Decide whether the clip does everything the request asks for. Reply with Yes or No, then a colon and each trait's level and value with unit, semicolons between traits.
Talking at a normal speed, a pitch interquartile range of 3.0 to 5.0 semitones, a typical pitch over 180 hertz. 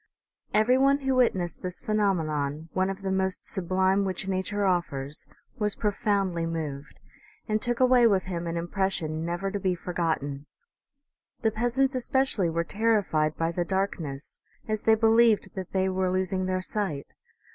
Yes: average, 160 wpm; average, 4.1 semitones; high, 190 Hz